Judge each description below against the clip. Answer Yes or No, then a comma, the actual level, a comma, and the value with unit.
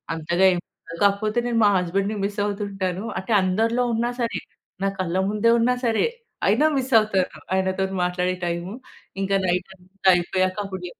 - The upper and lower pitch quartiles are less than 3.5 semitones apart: Yes, average, 2.8 semitones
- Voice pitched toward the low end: No, high, 195 Hz